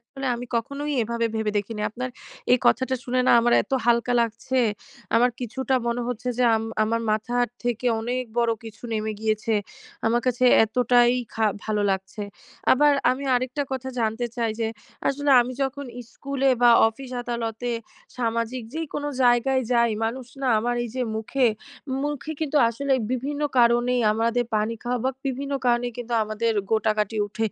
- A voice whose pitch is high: Yes, high, 240 Hz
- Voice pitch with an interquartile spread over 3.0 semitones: No, narrow, 2.4 semitones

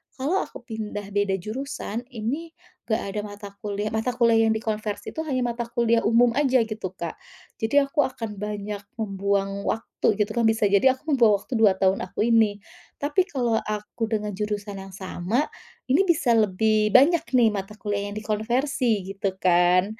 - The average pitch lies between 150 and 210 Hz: No, high, 220 Hz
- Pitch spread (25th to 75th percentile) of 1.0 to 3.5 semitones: Yes, average, 3.2 semitones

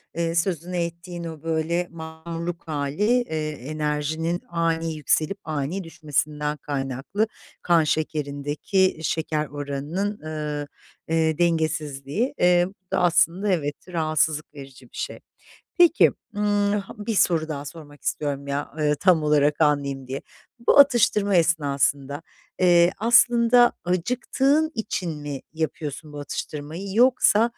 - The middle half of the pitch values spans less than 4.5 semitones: Yes, average, 3.5 semitones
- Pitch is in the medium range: Yes, medium, 160 Hz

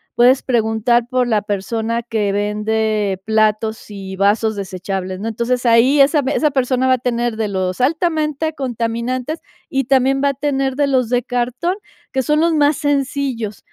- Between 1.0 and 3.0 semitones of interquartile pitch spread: No, average, 3.8 semitones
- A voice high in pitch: Yes, high, 240 Hz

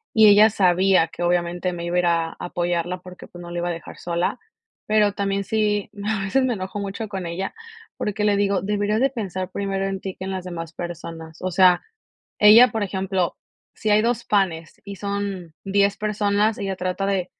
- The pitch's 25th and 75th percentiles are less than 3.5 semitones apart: Yes, average, 2.7 semitones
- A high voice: Yes, high, 195 Hz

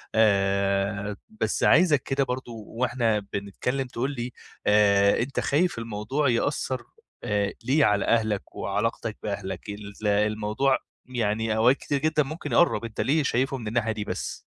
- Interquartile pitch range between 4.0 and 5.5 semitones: Yes, average, 4.3 semitones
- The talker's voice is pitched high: No, low, 115 Hz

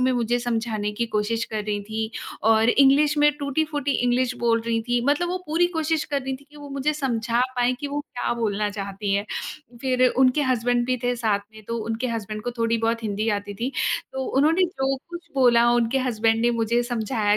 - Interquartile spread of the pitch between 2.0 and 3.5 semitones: Yes, average, 3.2 semitones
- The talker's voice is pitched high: Yes, high, 240 Hz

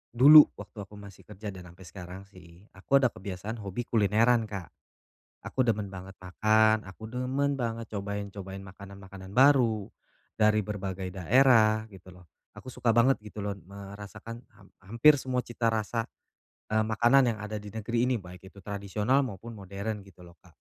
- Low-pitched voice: Yes, low, 105 Hz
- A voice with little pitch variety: No, average, 3.1 semitones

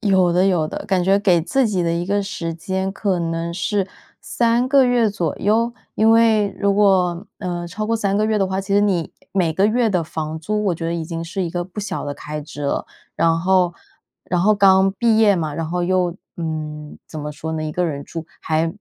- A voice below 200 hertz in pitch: Yes, medium, 185 Hz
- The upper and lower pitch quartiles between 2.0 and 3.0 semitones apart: No, average, 3.6 semitones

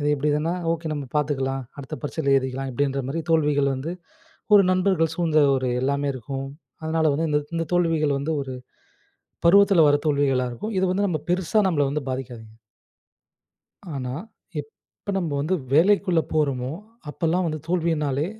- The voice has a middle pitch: Yes, medium, 150 Hz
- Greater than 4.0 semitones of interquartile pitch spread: No, average, 3.3 semitones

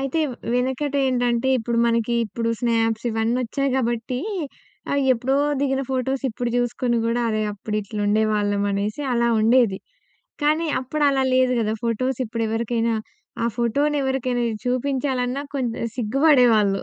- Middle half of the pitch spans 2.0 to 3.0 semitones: Yes, average, 2.7 semitones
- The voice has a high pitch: Yes, high, 240 Hz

